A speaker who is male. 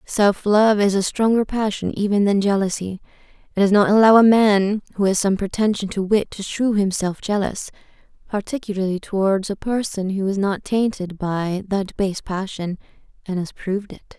No: female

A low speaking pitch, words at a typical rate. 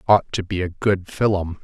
No: very low, 95 Hz; fast, 220 wpm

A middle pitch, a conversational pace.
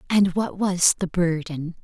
Yes: medium, 180 Hz; average, 165 wpm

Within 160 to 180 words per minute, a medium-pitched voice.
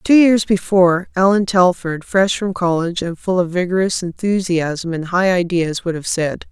Yes: average, 175 wpm; medium, 180 Hz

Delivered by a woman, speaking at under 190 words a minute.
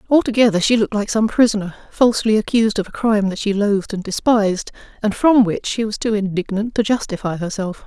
No: female; average, 200 wpm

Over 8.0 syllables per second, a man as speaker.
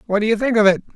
Yes: 8.5 syllables/s; male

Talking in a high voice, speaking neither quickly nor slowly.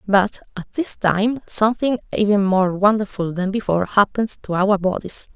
Yes: high, 200 Hz; average, 155 wpm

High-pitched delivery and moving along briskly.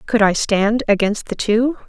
No: high, 225 Hz; average, 190 wpm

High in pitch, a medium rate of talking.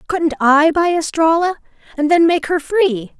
Yes: very high, 320 Hz; average, 170 wpm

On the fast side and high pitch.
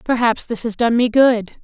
Yes: fast, 220 wpm; high, 235 Hz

